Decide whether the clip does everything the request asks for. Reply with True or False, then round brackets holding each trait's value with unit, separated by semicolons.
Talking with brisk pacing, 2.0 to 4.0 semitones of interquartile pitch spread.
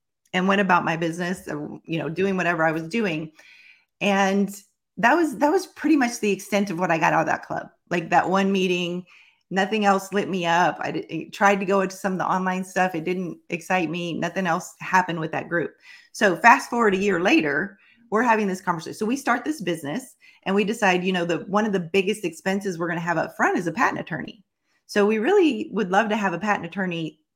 True (230 wpm; 3.2 semitones)